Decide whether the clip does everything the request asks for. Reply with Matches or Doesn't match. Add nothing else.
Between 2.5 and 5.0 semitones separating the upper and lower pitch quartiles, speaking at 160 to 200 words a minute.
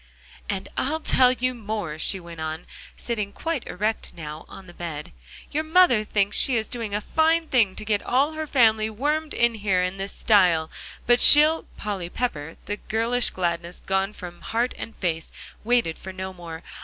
Doesn't match